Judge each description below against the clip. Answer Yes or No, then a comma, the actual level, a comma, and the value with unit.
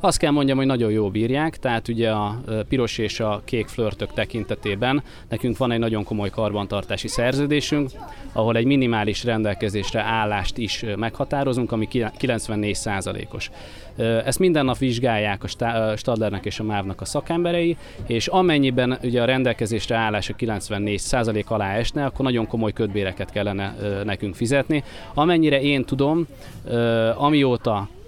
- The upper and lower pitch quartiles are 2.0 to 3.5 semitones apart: No, average, 3.9 semitones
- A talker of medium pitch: No, low, 115 Hz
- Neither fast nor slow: Yes, average, 140 wpm